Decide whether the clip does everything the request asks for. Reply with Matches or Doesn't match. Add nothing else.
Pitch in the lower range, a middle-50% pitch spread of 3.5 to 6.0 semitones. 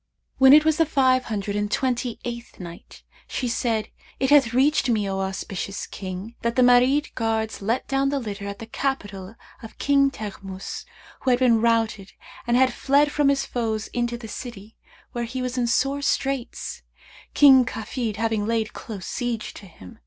Doesn't match